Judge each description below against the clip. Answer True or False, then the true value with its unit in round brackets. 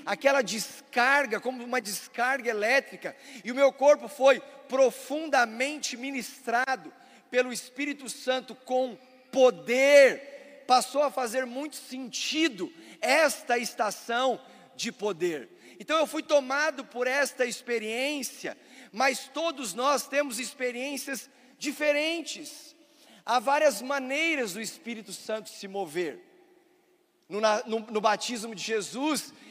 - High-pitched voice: True (260 Hz)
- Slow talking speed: True (110 wpm)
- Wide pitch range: False (3.0 semitones)